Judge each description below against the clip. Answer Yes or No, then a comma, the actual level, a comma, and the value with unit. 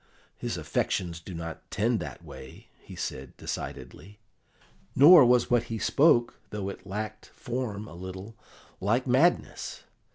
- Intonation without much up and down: No, average, 4.7 semitones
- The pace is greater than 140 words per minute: No, slow, 135 wpm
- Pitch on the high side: No, low, 110 Hz